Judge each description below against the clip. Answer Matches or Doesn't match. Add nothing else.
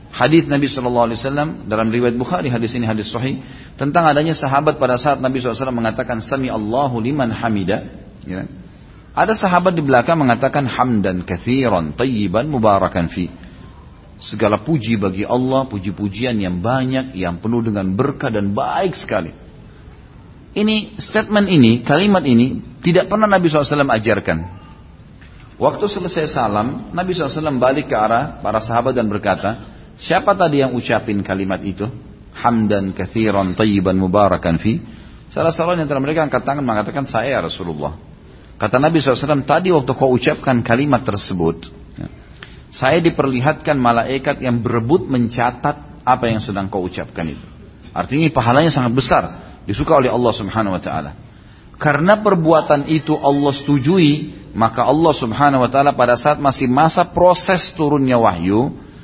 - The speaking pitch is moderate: Doesn't match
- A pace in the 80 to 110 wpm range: Doesn't match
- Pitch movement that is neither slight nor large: Doesn't match